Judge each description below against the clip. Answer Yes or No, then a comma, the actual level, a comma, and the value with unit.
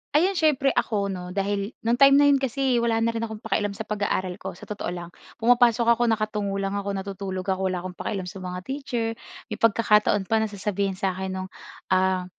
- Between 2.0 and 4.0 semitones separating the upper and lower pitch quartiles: Yes, average, 3.6 semitones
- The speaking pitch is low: No, high, 205 Hz